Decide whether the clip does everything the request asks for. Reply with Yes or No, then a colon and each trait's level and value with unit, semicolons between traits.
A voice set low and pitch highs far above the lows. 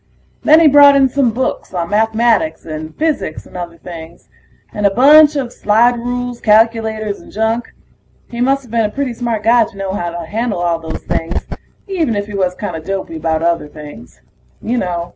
No: high, 215 Hz; wide, 6.1 semitones